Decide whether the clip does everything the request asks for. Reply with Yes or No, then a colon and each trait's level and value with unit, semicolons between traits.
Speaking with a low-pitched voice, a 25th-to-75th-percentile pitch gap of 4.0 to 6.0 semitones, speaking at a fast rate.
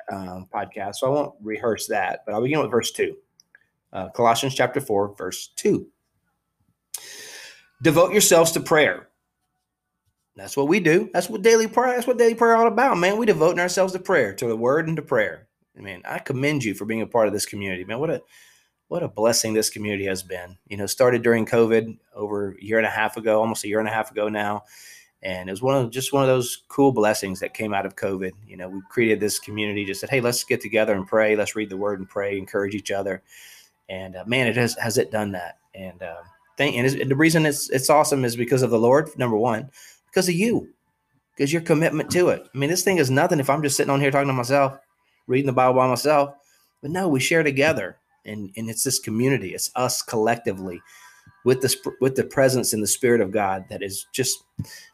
Yes: low, 120 Hz; wide, 5.4 semitones; fast, 230 wpm